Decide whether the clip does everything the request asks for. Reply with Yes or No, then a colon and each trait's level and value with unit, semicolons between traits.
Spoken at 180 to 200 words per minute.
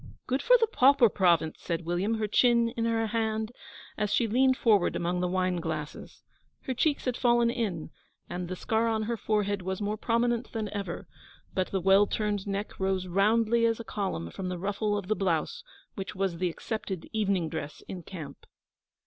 Yes: average, 190 wpm